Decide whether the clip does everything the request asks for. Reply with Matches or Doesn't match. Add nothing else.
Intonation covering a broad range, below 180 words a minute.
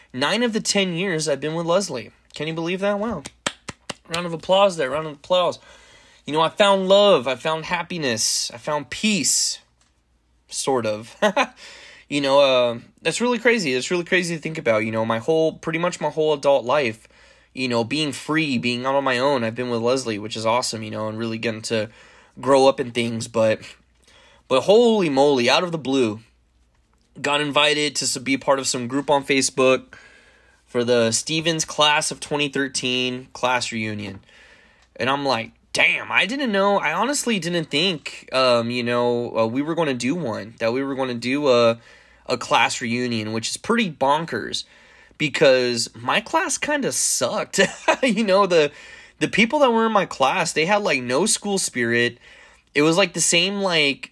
Doesn't match